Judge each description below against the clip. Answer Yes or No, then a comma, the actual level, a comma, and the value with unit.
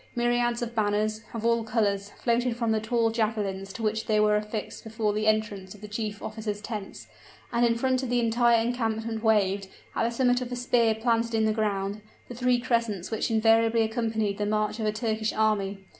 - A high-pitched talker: Yes, high, 220 Hz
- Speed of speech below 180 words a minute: No, fast, 205 wpm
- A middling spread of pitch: No, narrow, 1.7 semitones